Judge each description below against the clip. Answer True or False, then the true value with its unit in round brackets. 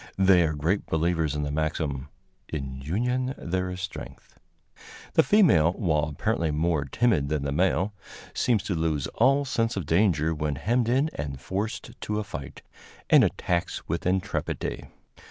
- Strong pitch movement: True (5.8 semitones)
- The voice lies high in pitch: False (85 Hz)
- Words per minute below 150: False (155 wpm)